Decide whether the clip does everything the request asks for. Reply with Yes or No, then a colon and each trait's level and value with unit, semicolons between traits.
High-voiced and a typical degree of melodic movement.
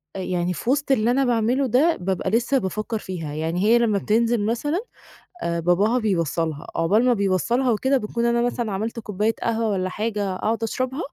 Yes: high, 220 Hz; average, 4.2 semitones